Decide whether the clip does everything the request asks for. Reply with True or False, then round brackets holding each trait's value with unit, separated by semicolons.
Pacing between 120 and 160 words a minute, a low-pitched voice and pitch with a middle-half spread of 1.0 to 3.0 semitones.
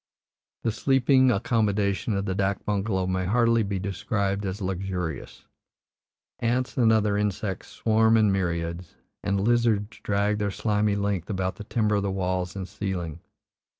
True (150 wpm; 100 Hz; 2.4 semitones)